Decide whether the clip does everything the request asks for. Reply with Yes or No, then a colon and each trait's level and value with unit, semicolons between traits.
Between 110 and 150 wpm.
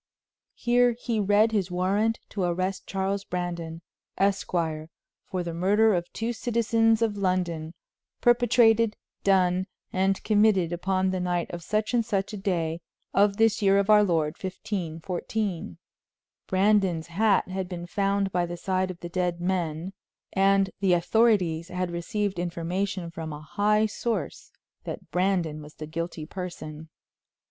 Yes: average, 145 wpm